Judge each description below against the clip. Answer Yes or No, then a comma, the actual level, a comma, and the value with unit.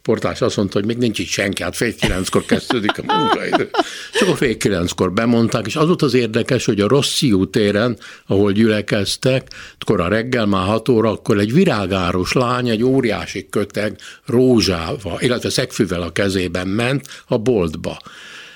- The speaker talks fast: Yes, fast, 165 wpm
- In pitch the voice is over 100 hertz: Yes, low, 110 Hz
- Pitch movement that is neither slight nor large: Yes, average, 4.2 semitones